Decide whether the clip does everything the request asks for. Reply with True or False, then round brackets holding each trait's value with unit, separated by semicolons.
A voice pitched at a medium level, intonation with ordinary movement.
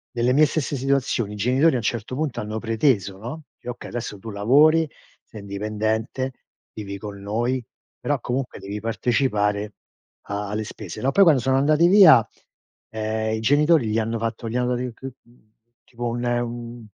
False (120 Hz; 3.5 semitones)